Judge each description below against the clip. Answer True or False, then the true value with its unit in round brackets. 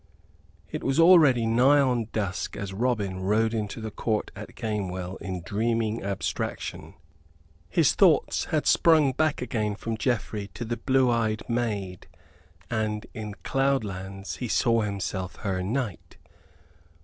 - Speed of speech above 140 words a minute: False (135 wpm)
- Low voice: True (110 Hz)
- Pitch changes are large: False (3.8 semitones)